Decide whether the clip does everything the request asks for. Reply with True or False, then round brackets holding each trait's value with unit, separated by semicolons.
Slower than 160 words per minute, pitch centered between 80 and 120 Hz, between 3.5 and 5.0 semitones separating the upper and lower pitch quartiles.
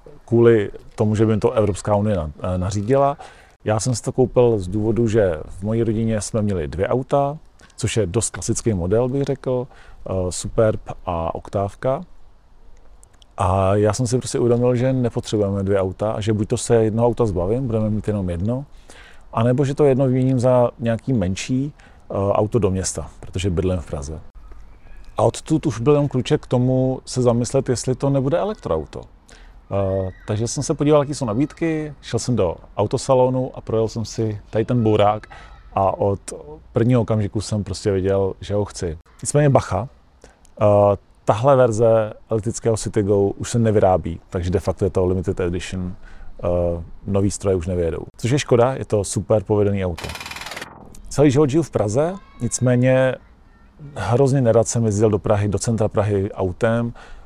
False (165 wpm; 110 Hz; 4.3 semitones)